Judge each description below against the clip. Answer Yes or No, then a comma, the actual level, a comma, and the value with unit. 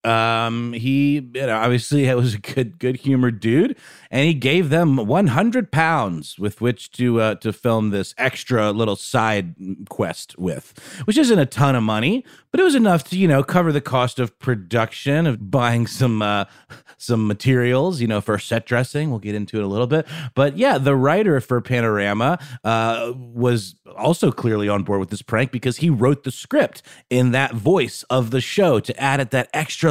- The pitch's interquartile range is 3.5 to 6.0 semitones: Yes, average, 4.0 semitones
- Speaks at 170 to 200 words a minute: Yes, average, 195 wpm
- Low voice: Yes, low, 125 Hz